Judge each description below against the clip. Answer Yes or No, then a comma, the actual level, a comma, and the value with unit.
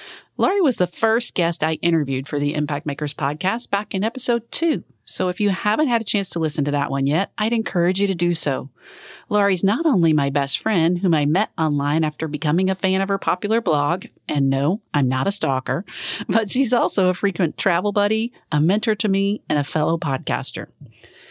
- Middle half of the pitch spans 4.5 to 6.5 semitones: Yes, wide, 5.6 semitones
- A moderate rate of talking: No, fast, 210 wpm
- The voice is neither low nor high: Yes, medium, 180 Hz